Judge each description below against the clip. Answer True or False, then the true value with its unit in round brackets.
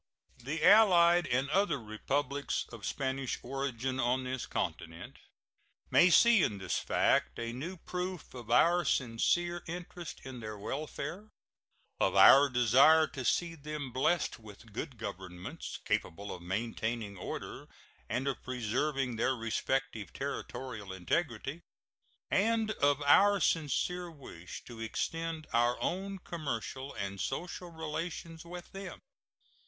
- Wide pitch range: True (6.5 semitones)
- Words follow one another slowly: True (125 wpm)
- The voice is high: False (135 Hz)